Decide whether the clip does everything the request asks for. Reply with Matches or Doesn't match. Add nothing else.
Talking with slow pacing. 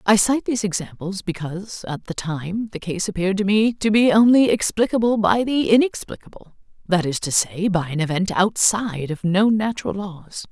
Doesn't match